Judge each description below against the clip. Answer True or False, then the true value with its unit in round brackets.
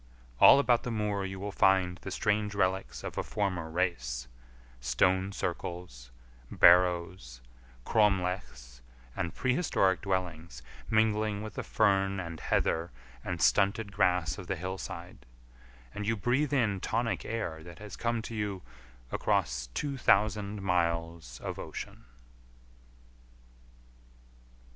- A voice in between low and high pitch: False (95 Hz)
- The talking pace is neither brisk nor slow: False (120 wpm)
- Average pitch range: True (3.5 semitones)